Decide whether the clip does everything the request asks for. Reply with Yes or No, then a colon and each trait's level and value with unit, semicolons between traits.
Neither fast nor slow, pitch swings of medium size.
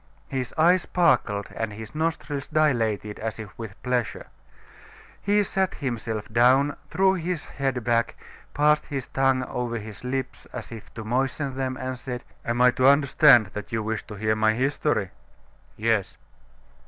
Yes: average, 155 wpm; average, 4.1 semitones